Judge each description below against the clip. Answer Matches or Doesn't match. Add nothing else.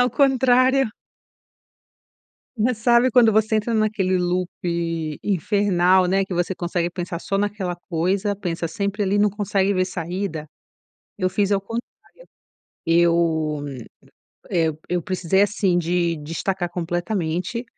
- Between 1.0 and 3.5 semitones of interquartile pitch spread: Matches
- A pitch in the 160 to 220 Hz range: Matches